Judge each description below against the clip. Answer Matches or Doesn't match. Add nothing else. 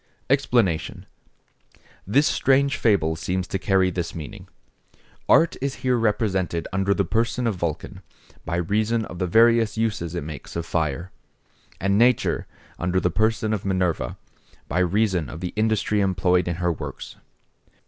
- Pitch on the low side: Matches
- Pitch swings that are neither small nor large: Matches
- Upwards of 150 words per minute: Doesn't match